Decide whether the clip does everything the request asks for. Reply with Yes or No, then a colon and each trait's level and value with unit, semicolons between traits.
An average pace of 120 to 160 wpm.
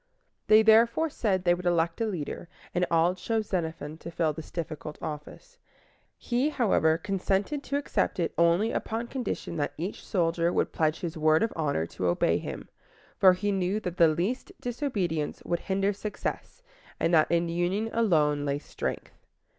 No: average, 170 wpm